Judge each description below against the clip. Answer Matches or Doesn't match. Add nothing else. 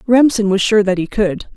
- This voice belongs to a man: Doesn't match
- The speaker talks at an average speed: Doesn't match